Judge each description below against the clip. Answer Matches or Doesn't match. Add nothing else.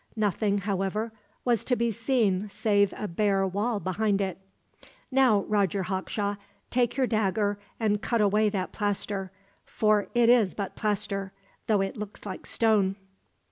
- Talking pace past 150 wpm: Doesn't match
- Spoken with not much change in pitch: Matches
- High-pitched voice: Matches